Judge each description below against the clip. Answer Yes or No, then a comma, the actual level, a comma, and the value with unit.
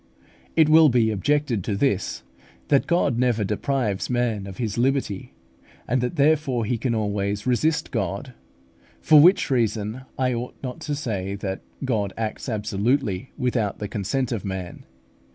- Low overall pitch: Yes, low, 120 Hz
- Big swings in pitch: No, average, 4.8 semitones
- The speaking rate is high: No, average, 150 wpm